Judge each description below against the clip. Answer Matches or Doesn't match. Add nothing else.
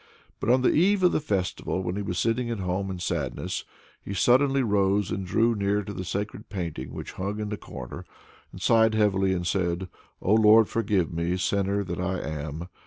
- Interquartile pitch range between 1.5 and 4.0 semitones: Matches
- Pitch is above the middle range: Doesn't match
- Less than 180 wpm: Doesn't match